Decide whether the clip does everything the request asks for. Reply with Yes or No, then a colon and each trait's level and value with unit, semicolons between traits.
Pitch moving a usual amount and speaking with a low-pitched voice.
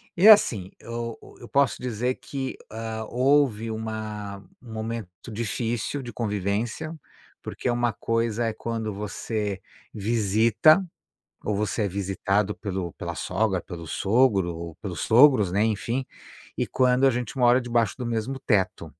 Yes: average, 3.1 semitones; low, 110 Hz